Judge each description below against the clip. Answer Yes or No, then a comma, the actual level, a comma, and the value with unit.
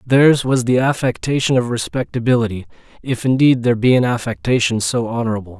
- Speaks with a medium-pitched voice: No, low, 120 Hz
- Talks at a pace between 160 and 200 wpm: No, average, 140 wpm